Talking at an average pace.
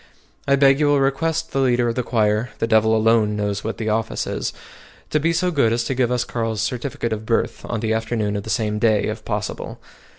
No: fast, 230 wpm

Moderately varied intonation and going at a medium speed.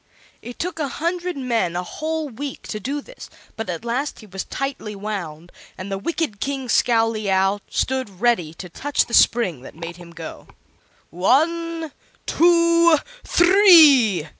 No: wide, 8.6 semitones; average, 150 wpm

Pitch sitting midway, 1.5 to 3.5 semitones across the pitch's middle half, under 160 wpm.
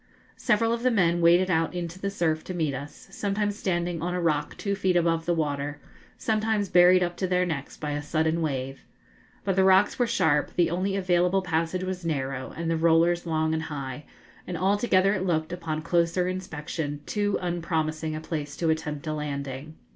No: medium, 170 Hz; average, 3.1 semitones; average, 195 wpm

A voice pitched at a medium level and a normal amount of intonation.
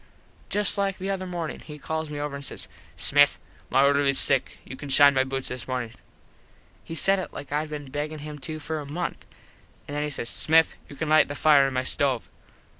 No: medium, 145 Hz; narrow, 2.3 semitones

